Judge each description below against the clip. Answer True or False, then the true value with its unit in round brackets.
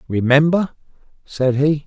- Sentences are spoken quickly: False (95 wpm)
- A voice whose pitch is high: False (145 Hz)